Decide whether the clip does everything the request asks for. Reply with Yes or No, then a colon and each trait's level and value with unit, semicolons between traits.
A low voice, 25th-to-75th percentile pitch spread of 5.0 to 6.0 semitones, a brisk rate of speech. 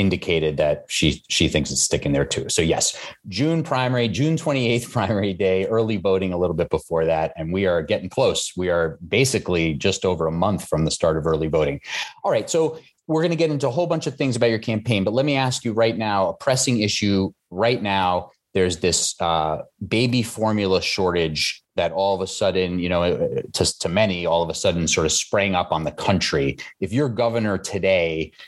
Yes: low, 100 Hz; wide, 5.4 semitones; fast, 215 wpm